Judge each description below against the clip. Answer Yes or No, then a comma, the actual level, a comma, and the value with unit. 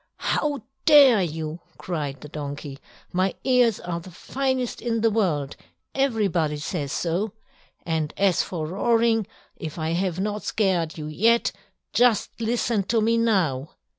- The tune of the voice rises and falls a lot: Yes, wide, 6.4 semitones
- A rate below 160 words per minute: Yes, average, 140 wpm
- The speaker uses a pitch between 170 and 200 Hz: Yes, high, 190 Hz